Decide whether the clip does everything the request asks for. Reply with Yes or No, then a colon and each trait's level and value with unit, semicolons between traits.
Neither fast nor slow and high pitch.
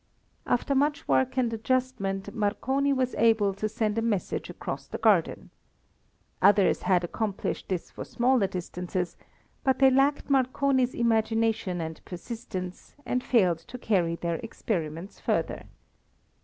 No: slow, 130 wpm; high, 220 Hz